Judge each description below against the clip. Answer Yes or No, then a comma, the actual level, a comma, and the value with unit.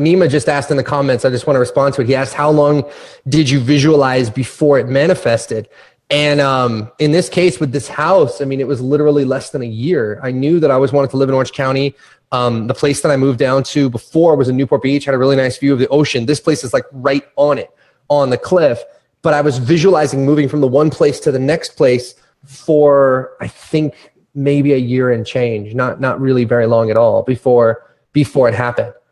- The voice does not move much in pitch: Yes, narrow, 2.3 semitones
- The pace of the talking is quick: Yes, fast, 235 wpm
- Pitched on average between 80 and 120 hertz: No, medium, 140 Hz